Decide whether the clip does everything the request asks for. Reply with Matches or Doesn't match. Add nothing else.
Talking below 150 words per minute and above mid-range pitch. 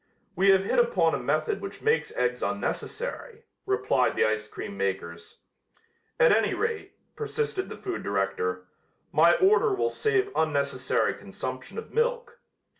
Matches